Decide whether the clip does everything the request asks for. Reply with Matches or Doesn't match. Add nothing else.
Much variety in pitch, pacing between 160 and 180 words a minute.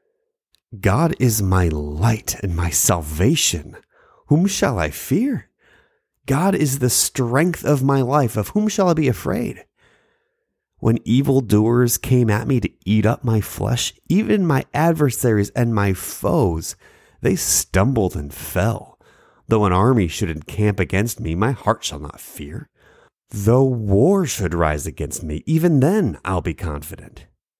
Doesn't match